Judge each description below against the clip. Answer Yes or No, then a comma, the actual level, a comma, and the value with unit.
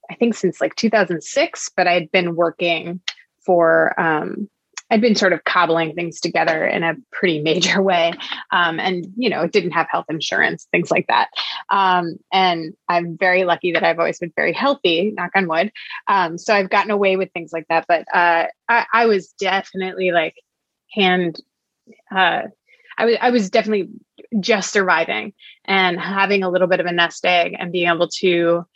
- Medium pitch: Yes, medium, 180 Hz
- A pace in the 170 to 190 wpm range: Yes, average, 180 wpm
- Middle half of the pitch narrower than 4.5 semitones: Yes, average, 2.8 semitones